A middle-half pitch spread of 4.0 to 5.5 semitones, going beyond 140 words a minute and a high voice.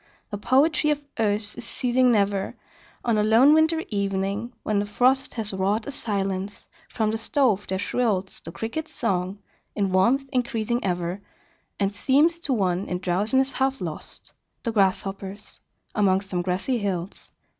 Yes: average, 4.5 semitones; average, 155 wpm; high, 210 Hz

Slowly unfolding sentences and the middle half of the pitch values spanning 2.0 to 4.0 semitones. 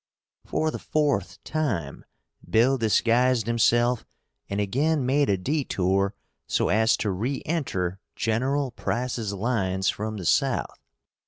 No: slow, 120 wpm; average, 5.2 semitones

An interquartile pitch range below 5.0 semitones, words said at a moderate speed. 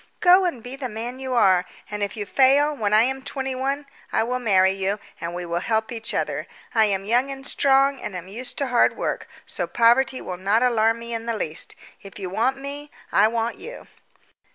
No: average, 4.4 semitones; fast, 220 wpm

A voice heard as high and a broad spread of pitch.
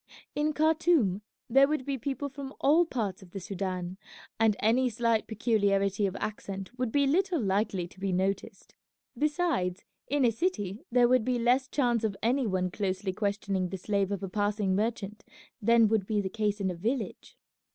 No: high, 215 Hz; average, 4.7 semitones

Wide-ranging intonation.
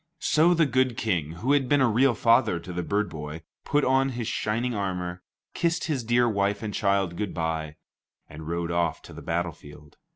Yes: wide, 6.8 semitones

